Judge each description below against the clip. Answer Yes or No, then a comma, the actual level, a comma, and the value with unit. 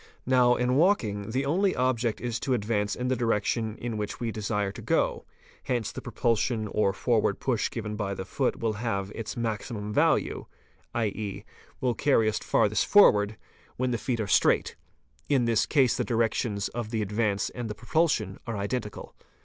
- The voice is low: Yes, low, 115 Hz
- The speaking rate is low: No, average, 175 wpm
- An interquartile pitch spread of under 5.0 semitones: Yes, average, 2.8 semitones